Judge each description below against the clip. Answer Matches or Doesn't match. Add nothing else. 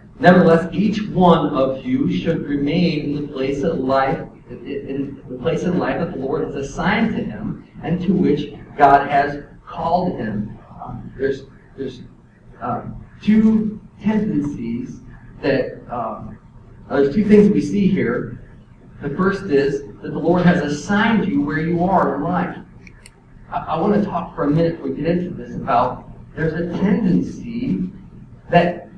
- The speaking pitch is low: Doesn't match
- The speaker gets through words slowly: Doesn't match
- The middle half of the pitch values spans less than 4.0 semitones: Doesn't match